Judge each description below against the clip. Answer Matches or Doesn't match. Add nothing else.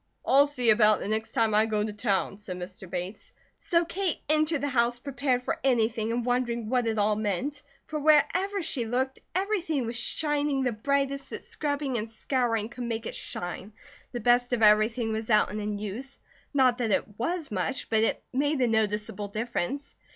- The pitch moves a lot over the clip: Doesn't match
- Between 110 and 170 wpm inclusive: Doesn't match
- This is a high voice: Matches